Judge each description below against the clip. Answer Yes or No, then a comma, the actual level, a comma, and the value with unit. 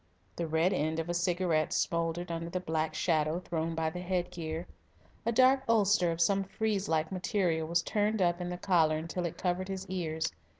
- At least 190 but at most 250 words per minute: Yes, average, 195 wpm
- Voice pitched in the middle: Yes, medium, 175 Hz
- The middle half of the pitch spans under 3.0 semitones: Yes, narrow, 2.5 semitones